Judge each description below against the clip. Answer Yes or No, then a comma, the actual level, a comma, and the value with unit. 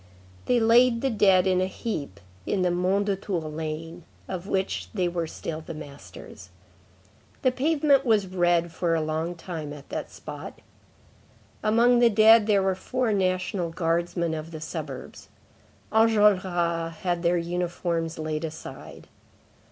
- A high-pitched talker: No, medium, 180 Hz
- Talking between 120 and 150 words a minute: Yes, average, 140 wpm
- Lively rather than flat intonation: No, average, 4.0 semitones